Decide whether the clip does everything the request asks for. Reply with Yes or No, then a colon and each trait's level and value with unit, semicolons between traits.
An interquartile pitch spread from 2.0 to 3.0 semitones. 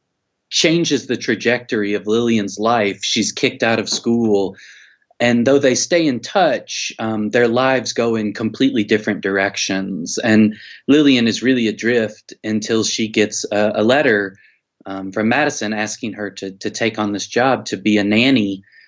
Yes: narrow, 2.5 semitones